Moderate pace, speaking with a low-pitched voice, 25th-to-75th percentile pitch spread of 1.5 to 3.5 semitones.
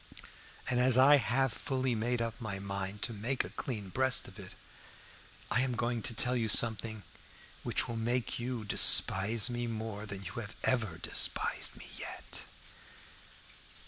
Yes: average, 155 wpm; low, 115 Hz; average, 2.7 semitones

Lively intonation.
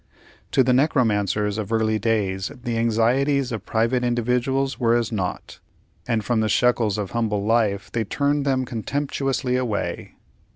No: average, 3.0 semitones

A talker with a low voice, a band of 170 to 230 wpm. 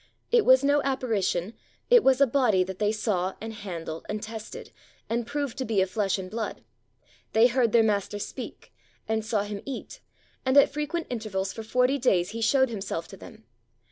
No: high, 220 Hz; average, 190 wpm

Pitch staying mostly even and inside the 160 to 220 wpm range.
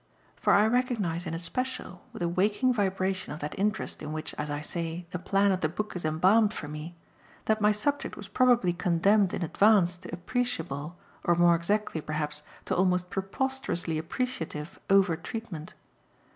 No: average, 4.3 semitones; average, 170 wpm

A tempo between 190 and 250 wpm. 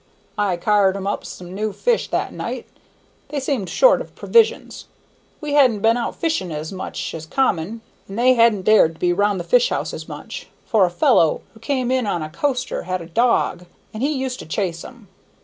Yes: average, 200 wpm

